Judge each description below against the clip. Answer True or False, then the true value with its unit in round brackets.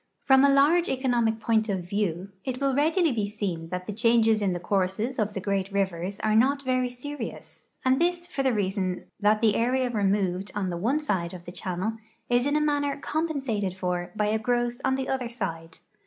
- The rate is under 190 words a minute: False (205 wpm)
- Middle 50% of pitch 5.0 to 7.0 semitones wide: True (5.4 semitones)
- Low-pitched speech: False (220 Hz)